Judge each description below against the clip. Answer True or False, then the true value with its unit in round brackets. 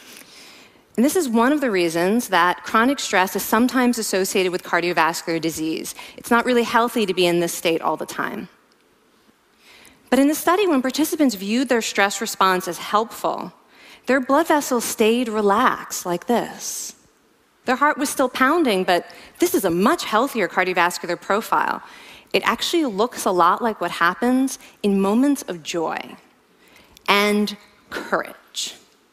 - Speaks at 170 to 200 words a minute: False (150 wpm)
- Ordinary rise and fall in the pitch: False (5.9 semitones)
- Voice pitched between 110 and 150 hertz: False (220 Hz)